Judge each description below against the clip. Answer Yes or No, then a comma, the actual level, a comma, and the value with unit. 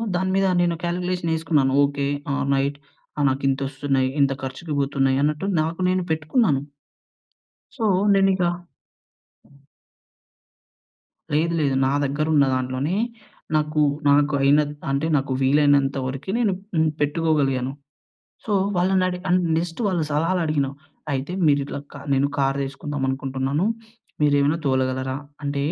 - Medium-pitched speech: Yes, medium, 145 Hz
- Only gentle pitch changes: No, average, 3.3 semitones